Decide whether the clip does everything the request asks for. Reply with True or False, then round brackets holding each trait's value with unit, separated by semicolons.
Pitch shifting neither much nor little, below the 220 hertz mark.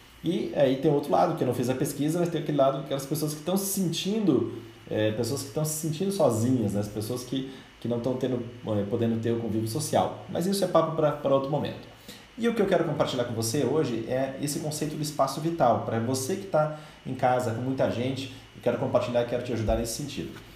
True (4.4 semitones; 135 Hz)